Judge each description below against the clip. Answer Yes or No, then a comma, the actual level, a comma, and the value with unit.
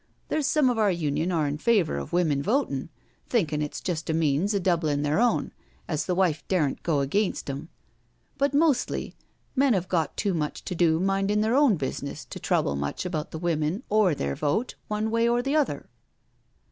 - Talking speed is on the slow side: No, average, 195 wpm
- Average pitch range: No, wide, 6.3 semitones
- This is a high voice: No, medium, 175 Hz